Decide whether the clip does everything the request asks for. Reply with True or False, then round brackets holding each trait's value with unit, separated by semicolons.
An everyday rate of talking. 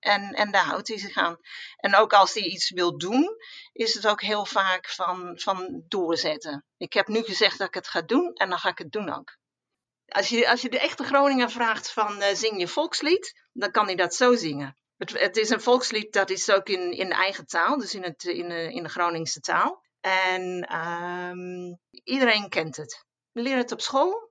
False (220 wpm)